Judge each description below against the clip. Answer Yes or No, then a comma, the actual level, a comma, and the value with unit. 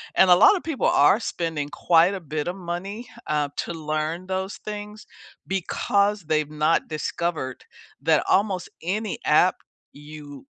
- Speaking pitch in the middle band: Yes, medium, 170 Hz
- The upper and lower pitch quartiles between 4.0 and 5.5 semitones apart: Yes, average, 4.4 semitones